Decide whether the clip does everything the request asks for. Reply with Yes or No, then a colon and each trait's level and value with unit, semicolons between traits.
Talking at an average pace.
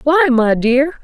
Yes: average, 175 wpm